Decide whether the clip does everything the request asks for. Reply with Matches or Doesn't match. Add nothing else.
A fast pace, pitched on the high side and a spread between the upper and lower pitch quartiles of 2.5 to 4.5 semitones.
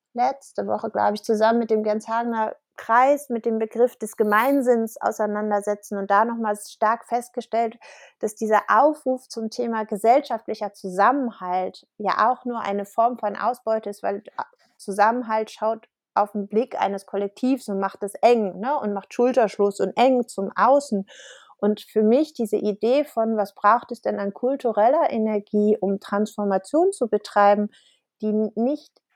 Doesn't match